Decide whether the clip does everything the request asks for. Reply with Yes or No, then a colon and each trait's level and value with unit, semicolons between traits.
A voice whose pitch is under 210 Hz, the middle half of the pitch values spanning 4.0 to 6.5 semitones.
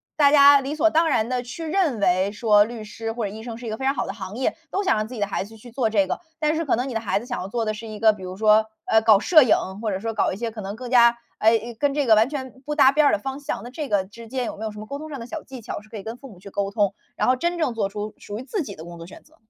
No: high, 230 Hz; average, 4.4 semitones